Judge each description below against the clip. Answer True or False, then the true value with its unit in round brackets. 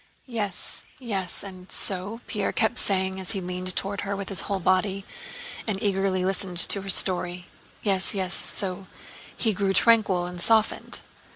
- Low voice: False (195 Hz)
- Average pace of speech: True (160 wpm)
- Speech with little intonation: True (1.6 semitones)